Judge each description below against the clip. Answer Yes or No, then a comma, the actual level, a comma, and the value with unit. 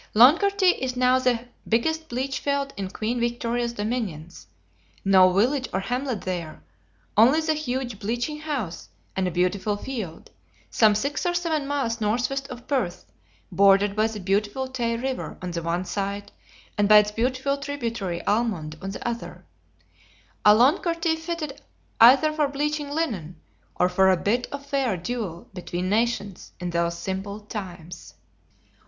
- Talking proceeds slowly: No, average, 150 wpm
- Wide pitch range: Yes, wide, 5.9 semitones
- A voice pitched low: No, high, 230 Hz